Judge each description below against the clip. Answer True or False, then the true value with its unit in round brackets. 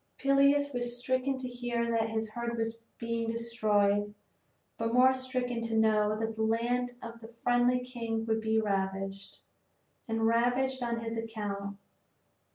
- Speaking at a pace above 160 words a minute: False (150 wpm)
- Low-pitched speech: False (230 Hz)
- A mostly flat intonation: True (1.8 semitones)